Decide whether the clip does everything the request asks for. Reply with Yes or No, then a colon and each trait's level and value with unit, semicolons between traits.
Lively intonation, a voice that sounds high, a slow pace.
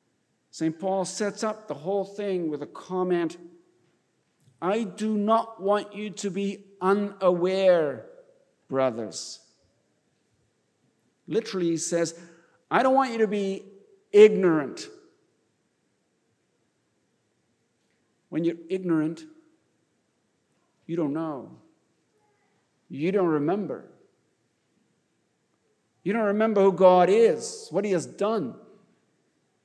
No: average, 4.5 semitones; high, 195 Hz; slow, 95 wpm